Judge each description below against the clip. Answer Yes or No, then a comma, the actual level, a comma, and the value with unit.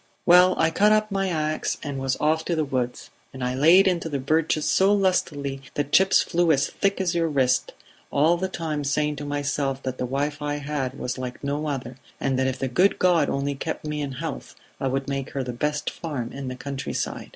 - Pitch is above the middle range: No, medium, 145 Hz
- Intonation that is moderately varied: Yes, average, 3.5 semitones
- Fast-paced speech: Yes, fast, 220 wpm